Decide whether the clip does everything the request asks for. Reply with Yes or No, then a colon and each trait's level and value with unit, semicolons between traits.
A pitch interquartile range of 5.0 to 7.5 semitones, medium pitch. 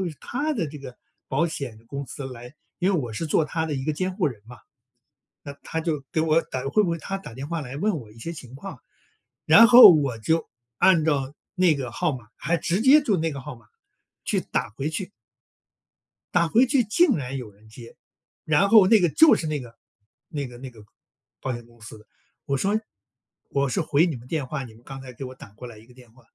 Yes: average, 5.3 semitones; medium, 145 Hz